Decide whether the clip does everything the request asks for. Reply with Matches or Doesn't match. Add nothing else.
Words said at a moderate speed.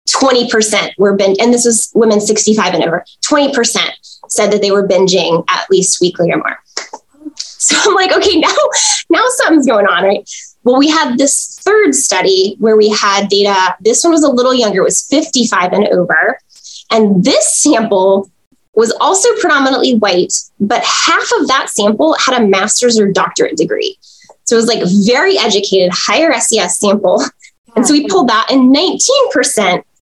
Matches